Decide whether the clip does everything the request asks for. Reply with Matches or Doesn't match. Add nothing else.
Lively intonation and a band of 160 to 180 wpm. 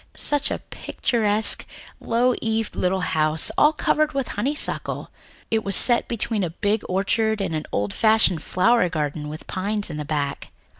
Matches